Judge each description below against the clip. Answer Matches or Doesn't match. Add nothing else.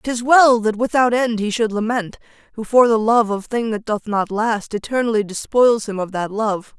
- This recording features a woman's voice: Matches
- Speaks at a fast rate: Matches